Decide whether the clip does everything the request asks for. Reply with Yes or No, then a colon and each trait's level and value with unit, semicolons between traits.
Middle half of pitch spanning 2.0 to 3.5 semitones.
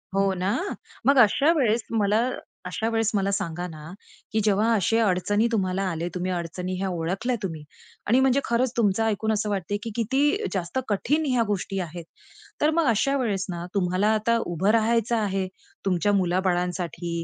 No: average, 4.0 semitones